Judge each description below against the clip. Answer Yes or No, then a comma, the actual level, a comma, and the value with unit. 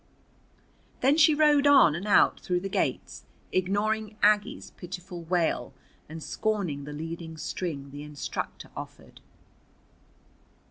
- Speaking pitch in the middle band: Yes, medium, 180 Hz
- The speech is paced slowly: Yes, slow, 120 wpm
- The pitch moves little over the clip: No, average, 4.9 semitones